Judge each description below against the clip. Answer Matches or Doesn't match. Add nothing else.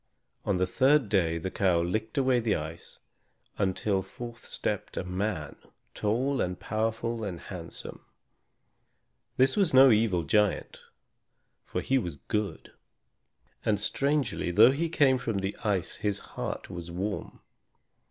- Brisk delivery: Doesn't match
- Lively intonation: Doesn't match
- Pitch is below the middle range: Matches